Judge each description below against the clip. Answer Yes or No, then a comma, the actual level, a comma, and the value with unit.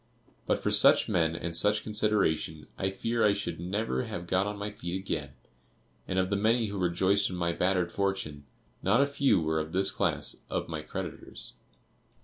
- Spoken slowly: No, average, 185 wpm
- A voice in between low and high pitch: No, very low, 95 Hz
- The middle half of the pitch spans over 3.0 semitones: Yes, average, 3.4 semitones